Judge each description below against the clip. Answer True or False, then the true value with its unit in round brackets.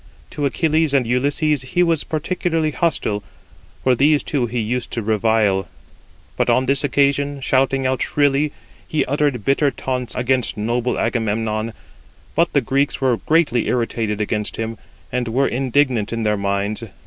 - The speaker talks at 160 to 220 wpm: False (150 wpm)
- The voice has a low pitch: True (130 Hz)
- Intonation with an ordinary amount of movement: True (4.0 semitones)